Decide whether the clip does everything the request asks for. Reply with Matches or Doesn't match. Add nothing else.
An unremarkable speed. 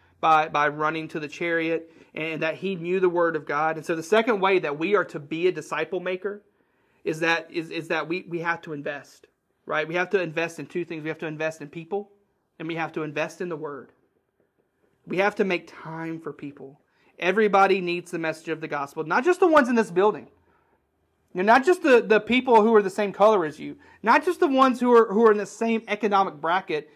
Doesn't match